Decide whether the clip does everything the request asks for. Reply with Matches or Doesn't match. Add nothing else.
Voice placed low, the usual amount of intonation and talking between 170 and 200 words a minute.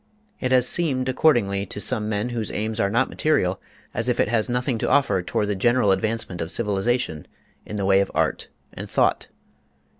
Matches